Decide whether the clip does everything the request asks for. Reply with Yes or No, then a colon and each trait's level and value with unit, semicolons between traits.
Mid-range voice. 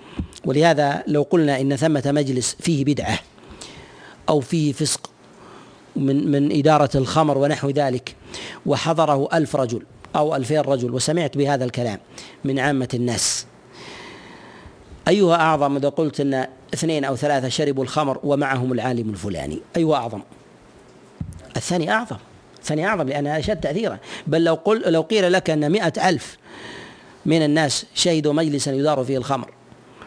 Yes: medium, 145 Hz